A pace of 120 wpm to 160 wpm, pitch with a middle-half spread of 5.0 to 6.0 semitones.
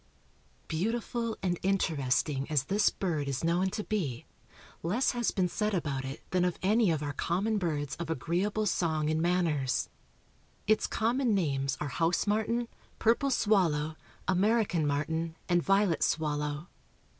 Yes: average, 145 wpm; wide, 5.6 semitones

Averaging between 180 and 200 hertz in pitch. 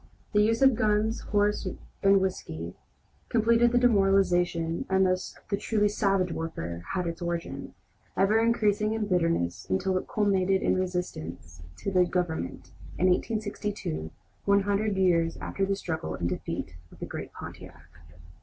Yes: high, 190 Hz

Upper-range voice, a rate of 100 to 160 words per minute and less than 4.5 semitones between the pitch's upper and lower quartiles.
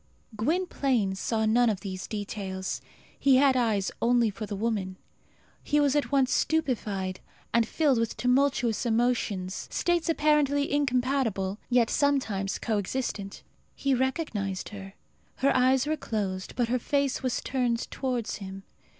No: high, 240 Hz; average, 140 wpm; average, 5.0 semitones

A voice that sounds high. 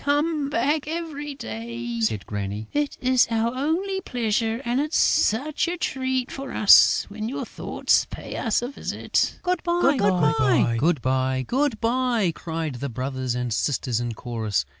Yes: high, 225 Hz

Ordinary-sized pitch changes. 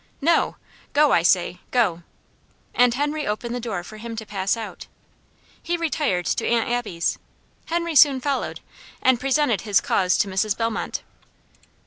No: wide, 6.2 semitones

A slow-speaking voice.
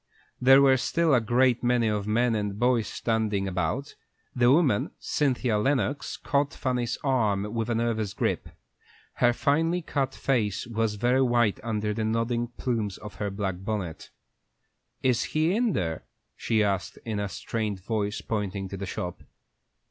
No: average, 155 wpm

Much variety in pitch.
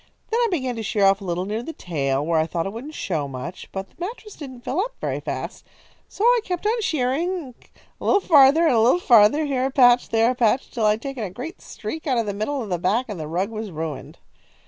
Yes: wide, 7.5 semitones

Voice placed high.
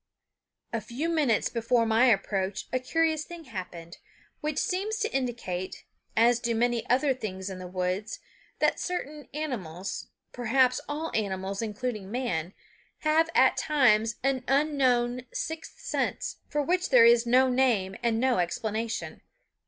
Yes: high, 240 Hz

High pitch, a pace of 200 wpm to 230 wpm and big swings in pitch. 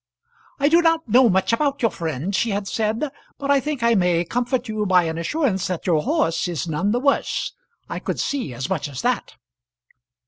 Yes: high, 215 Hz; fast, 205 wpm; wide, 7.4 semitones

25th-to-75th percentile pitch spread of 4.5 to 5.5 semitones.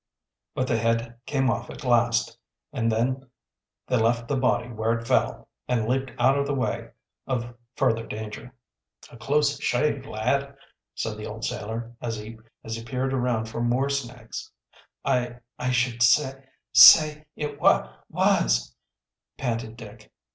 No: average, 2.7 semitones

